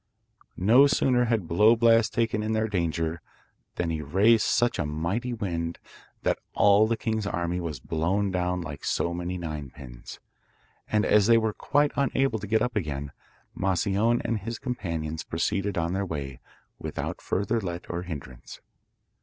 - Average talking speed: Yes, average, 160 wpm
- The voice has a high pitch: No, very low, 95 Hz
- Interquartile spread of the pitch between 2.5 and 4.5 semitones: No, average, 5.1 semitones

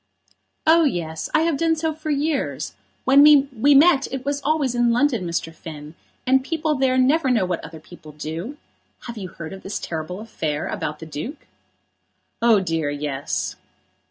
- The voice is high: Yes, high, 240 Hz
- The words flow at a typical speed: Yes, average, 170 wpm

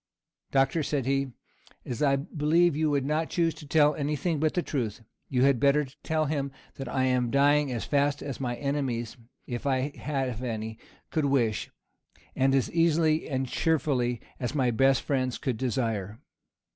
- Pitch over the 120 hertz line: Yes, medium, 140 Hz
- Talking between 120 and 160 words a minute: No, average, 170 wpm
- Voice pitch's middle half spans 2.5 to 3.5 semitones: Yes, average, 2.8 semitones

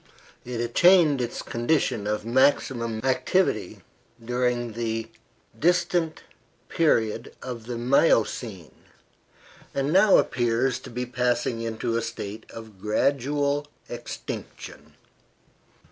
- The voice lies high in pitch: No, low, 120 Hz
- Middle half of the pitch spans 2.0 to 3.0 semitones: No, average, 3.6 semitones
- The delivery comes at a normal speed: No, slow, 100 wpm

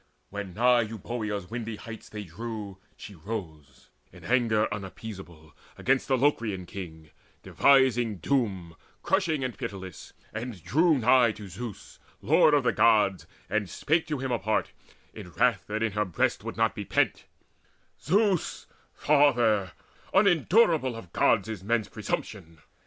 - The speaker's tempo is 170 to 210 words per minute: No, average, 140 wpm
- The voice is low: Yes, low, 110 Hz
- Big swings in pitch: No, average, 4.8 semitones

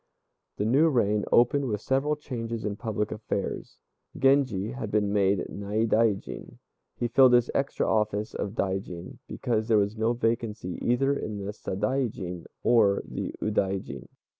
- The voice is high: No, low, 110 Hz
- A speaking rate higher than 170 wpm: No, average, 140 wpm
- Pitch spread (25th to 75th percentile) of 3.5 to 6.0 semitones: No, average, 3.1 semitones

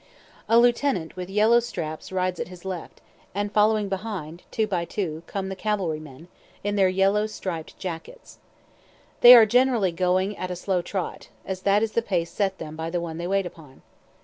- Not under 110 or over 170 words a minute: No, average, 190 wpm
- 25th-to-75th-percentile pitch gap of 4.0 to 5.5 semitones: No, average, 3.4 semitones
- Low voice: No, high, 190 Hz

